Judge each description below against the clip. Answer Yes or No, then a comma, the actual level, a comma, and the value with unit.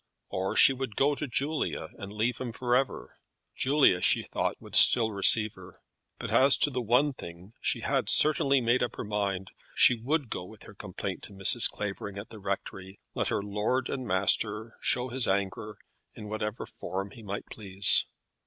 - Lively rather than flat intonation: No, average, 4.3 semitones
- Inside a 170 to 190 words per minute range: Yes, average, 180 wpm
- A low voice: Yes, low, 110 Hz